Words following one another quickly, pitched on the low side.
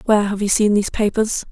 No: fast, 240 wpm; high, 210 Hz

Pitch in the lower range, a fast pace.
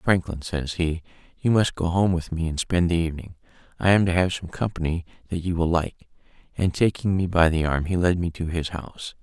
Yes: very low, 85 Hz; fast, 230 wpm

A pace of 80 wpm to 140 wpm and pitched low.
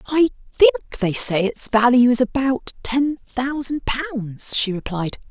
No: slow, 135 wpm; high, 245 Hz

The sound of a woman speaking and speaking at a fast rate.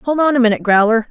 Yes: female; fast, 270 wpm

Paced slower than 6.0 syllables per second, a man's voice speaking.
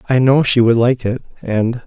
Yes: 4.9 syllables/s; male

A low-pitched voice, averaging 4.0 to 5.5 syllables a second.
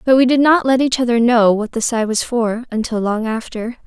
No: high, 240 Hz; 5.2 syllables/s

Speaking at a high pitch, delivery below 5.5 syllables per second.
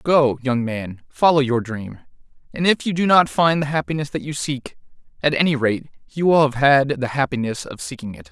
No: medium, 140 Hz; 5.1 syllables/s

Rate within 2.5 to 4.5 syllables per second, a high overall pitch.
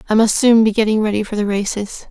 No: 6.3 syllables/s; high, 215 Hz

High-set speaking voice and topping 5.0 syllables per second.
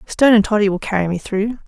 Yes: high, 205 Hz; 6.7 syllables/s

